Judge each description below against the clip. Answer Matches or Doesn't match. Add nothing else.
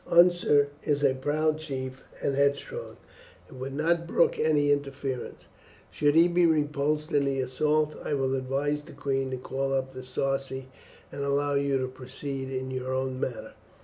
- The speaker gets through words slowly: Doesn't match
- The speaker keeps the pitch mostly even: Matches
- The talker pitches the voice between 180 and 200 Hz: Doesn't match